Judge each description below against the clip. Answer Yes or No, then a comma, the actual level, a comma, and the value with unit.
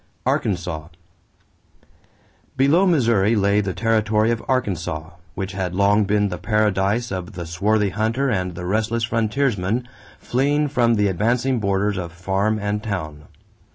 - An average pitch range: Yes, average, 3.6 semitones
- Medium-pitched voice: No, low, 105 Hz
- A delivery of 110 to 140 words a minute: Yes, slow, 135 wpm